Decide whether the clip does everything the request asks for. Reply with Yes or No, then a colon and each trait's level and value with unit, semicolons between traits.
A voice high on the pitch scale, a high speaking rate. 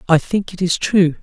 No: medium, 175 Hz; fast, 245 wpm